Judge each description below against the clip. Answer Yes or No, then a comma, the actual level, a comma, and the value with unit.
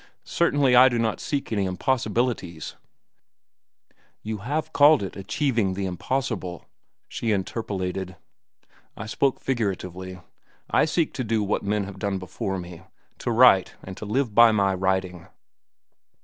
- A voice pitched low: Yes, low, 105 Hz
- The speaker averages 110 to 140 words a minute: Yes, slow, 135 wpm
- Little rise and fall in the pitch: No, average, 5.0 semitones